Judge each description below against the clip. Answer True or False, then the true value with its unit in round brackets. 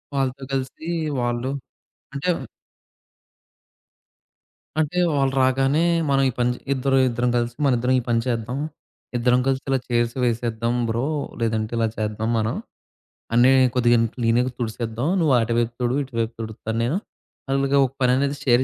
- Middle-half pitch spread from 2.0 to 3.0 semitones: True (2.4 semitones)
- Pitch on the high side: False (120 Hz)